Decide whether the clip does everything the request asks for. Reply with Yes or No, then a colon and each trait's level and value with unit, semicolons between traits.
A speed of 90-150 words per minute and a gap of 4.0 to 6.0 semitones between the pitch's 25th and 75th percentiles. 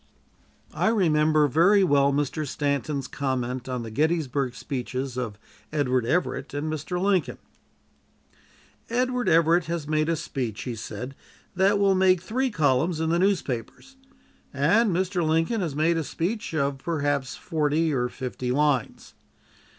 Yes: average, 140 wpm; average, 4.6 semitones